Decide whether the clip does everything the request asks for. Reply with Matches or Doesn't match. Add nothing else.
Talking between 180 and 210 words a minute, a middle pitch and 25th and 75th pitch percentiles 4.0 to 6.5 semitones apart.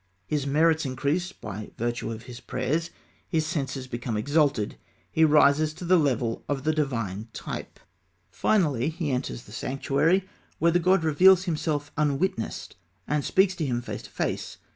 Doesn't match